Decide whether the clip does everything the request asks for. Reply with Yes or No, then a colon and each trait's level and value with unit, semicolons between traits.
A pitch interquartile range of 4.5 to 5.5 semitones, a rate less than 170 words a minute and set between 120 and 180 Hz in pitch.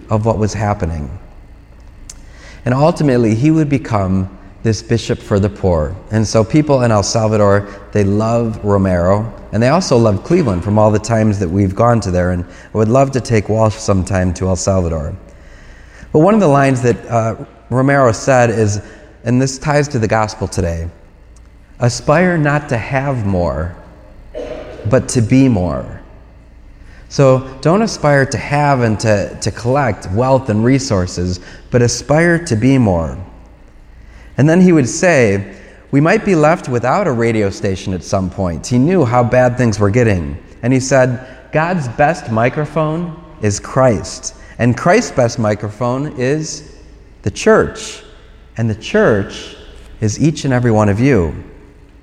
No: average, 5.2 semitones; average, 160 wpm; low, 110 Hz